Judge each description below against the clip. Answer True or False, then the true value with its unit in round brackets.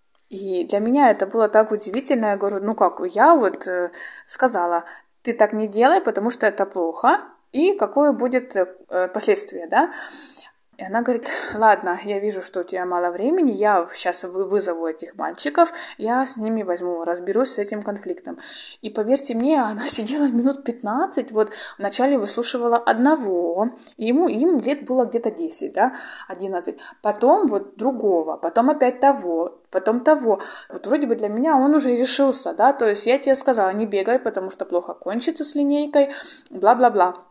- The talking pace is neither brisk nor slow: False (165 wpm)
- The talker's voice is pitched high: True (225 Hz)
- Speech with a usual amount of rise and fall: False (5.7 semitones)